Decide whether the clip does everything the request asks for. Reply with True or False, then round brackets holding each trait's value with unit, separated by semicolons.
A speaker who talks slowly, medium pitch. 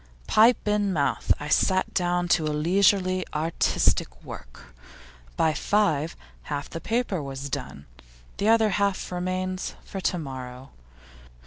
True (125 wpm; 180 Hz)